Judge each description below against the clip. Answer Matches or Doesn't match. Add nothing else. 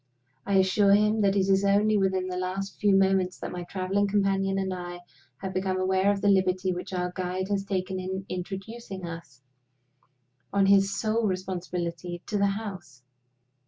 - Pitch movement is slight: Matches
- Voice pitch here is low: Doesn't match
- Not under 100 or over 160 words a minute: Doesn't match